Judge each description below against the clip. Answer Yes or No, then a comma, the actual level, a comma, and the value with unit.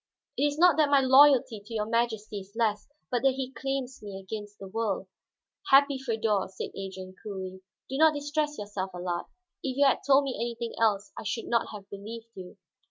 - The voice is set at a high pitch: Yes, high, 230 Hz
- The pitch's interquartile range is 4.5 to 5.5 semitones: Yes, average, 5.0 semitones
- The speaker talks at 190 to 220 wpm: Yes, average, 195 wpm